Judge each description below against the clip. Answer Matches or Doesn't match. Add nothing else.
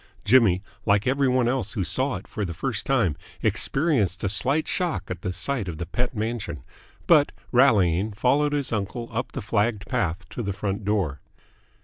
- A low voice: Matches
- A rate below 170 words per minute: Doesn't match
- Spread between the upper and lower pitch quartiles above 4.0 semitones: Matches